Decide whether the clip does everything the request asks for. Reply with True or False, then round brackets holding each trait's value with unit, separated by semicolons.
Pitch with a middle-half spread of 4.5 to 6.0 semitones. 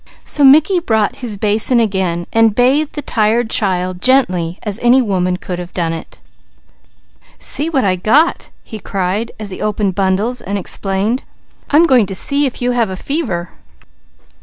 True (5.1 semitones)